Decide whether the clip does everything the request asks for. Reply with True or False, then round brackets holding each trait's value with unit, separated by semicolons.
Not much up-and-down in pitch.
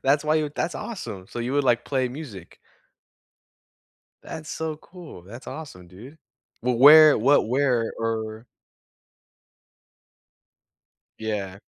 False (5.5 semitones)